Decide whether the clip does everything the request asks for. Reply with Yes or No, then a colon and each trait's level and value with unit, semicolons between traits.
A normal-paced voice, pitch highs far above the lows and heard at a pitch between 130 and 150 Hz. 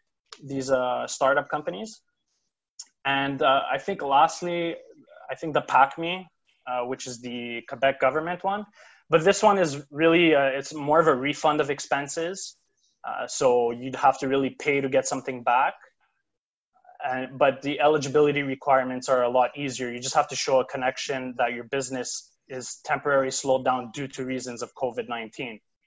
No: average, 165 wpm; average, 3.3 semitones; medium, 140 Hz